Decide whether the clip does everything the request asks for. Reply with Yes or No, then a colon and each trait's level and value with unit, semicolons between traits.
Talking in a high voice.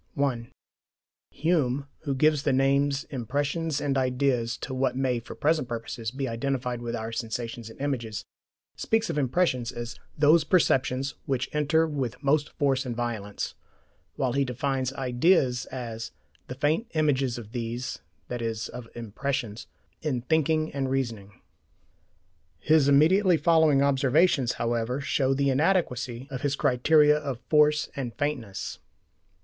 No: low, 135 Hz